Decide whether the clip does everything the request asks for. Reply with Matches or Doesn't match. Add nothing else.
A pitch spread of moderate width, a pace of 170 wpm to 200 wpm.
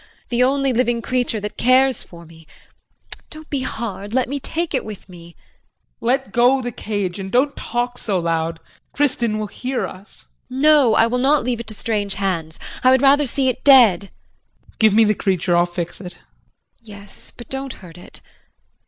Matches